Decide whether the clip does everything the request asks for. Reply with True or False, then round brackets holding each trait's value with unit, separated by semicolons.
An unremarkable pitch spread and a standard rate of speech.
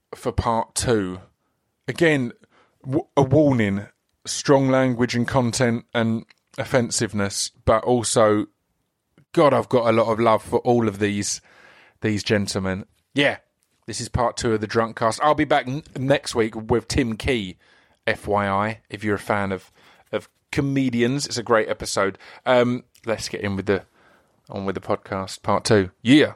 True (3.4 semitones; 160 wpm)